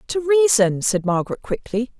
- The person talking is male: No, female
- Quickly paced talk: No, average, 150 wpm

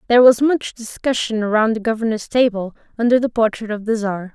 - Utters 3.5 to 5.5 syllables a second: No, 5.8 syllables/s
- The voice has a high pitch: Yes, high, 225 Hz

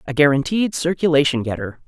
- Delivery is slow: Yes, slow, 130 wpm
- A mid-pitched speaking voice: Yes, medium, 145 Hz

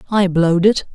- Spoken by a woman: Yes, female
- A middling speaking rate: Yes, average, 190 wpm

